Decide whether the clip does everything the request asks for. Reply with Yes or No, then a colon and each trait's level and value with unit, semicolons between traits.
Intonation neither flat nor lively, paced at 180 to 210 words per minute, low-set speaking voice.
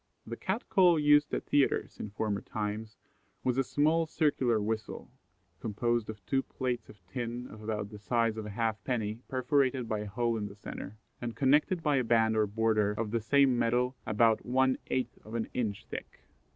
Yes: average, 3.4 semitones; average, 190 wpm; low, 115 Hz